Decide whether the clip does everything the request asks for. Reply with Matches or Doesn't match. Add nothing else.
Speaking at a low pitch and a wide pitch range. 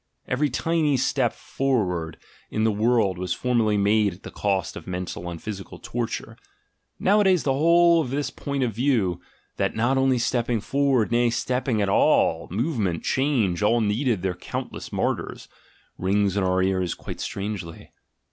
Matches